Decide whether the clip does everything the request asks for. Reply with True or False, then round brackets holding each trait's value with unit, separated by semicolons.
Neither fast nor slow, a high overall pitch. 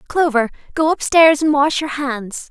True (190 wpm; 290 Hz)